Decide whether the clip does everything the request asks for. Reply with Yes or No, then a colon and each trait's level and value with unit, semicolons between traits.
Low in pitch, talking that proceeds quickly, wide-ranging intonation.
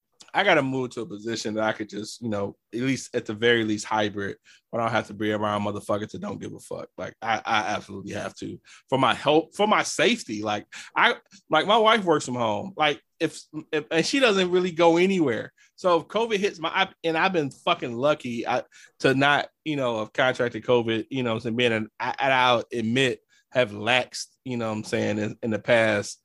Yes: low, 125 Hz; fast, 230 wpm; wide, 6.1 semitones